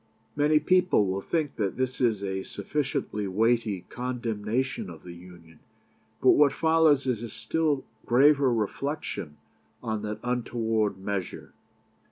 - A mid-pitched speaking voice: No, low, 115 Hz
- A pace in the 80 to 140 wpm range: Yes, slow, 135 wpm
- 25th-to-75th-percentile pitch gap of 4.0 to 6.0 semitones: Yes, wide, 5.4 semitones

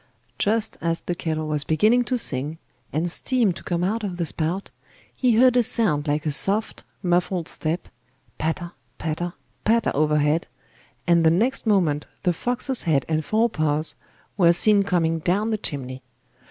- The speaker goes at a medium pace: Yes, average, 165 wpm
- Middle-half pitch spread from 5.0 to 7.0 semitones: Yes, wide, 5.4 semitones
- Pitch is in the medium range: Yes, medium, 175 Hz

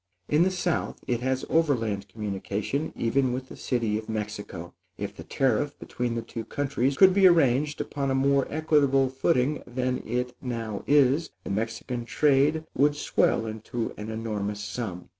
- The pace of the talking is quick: No, average, 160 wpm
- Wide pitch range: No, average, 4.3 semitones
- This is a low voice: Yes, low, 125 Hz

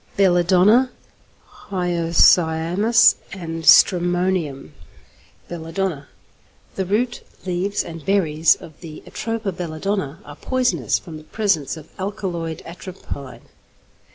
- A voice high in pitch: No, medium, 175 Hz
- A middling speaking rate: No, slow, 100 wpm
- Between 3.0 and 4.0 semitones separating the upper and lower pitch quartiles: Yes, average, 3.3 semitones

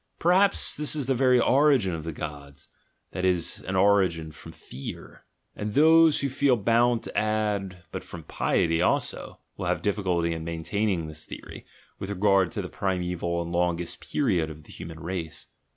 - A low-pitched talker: Yes, very low, 95 Hz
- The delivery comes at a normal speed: Yes, average, 170 wpm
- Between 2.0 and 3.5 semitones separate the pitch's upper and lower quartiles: No, wide, 5.5 semitones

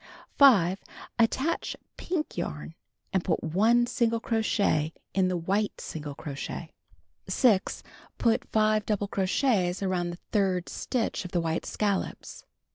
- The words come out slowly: Yes, slow, 125 wpm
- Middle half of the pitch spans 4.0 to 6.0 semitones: Yes, average, 4.3 semitones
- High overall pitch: Yes, high, 195 Hz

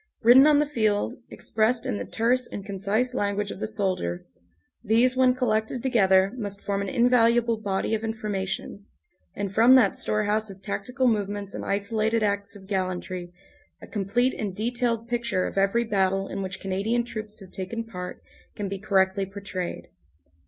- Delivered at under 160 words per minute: No, average, 165 wpm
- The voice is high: Yes, high, 210 Hz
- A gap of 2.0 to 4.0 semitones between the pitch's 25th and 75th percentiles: Yes, average, 3.0 semitones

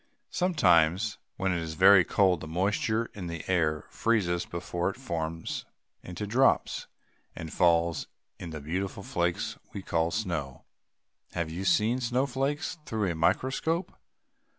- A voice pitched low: Yes, very low, 95 Hz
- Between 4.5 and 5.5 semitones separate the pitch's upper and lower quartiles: Yes, average, 5.0 semitones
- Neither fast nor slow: Yes, average, 145 wpm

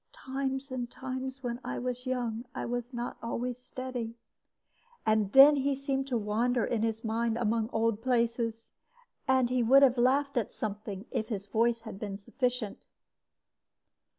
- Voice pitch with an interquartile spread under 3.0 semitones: Yes, narrow, 2.5 semitones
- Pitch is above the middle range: Yes, high, 240 Hz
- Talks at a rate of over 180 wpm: No, average, 155 wpm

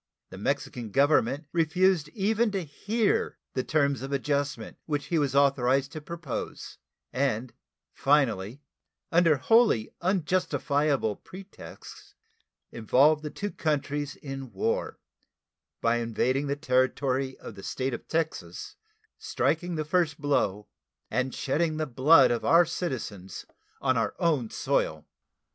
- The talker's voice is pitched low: No, medium, 145 Hz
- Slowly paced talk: Yes, slow, 125 wpm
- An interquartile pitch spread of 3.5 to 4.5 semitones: Yes, average, 3.9 semitones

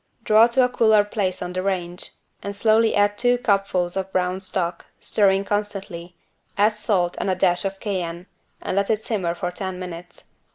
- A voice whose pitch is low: No, high, 195 Hz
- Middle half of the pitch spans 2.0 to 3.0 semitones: Yes, narrow, 2.6 semitones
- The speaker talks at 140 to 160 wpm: No, average, 175 wpm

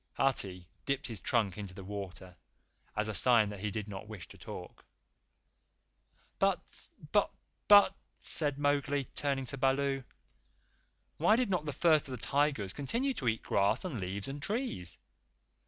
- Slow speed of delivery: No, average, 155 wpm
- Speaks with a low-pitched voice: Yes, low, 130 Hz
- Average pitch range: No, wide, 6.1 semitones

